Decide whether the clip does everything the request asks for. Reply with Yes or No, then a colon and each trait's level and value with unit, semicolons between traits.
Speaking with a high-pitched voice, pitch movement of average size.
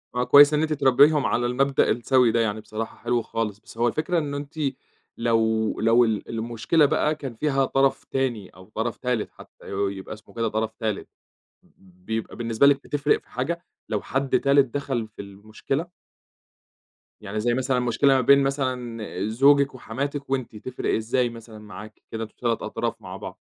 No: low, 120 Hz; average, 3.7 semitones